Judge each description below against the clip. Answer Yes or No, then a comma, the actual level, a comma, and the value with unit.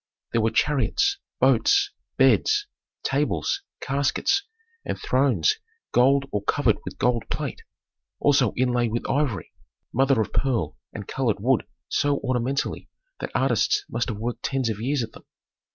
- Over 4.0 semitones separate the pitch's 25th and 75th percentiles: No, average, 3.5 semitones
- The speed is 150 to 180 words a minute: No, average, 140 wpm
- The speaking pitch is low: Yes, low, 130 Hz